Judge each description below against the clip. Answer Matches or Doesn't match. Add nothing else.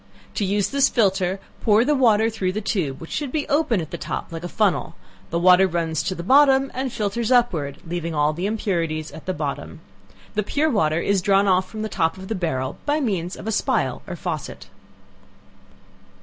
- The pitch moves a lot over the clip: Doesn't match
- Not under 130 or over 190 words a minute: Doesn't match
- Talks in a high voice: Matches